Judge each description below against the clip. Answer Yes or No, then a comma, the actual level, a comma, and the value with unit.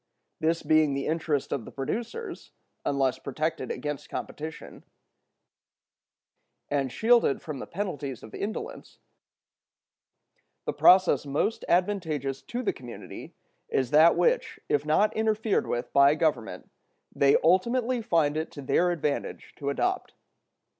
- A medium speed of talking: No, slow, 125 wpm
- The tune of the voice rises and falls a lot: Yes, wide, 6.5 semitones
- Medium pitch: Yes, medium, 155 Hz